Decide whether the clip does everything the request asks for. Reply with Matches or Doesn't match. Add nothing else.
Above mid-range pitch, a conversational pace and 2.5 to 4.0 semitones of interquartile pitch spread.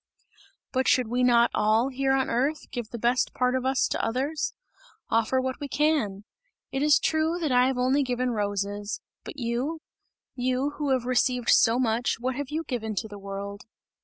Matches